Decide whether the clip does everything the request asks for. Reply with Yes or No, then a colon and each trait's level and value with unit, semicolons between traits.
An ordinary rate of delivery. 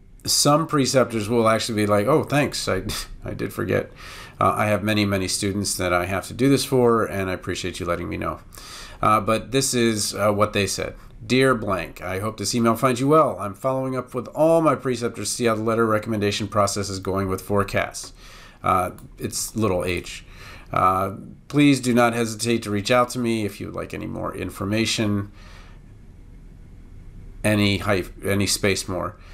Yes: average, 190 wpm